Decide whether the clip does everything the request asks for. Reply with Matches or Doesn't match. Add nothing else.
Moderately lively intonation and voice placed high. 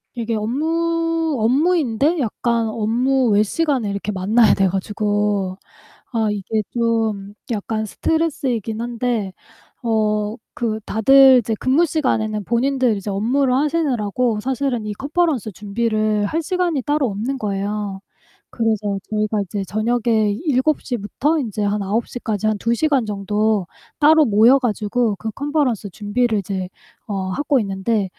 Matches